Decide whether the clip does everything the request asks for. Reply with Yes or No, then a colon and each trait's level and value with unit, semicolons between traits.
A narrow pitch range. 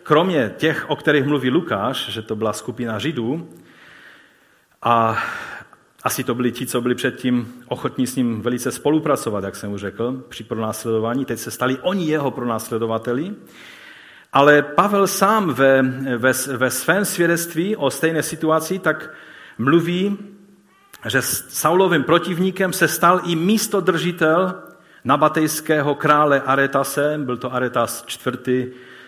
No: average, 4.8 semitones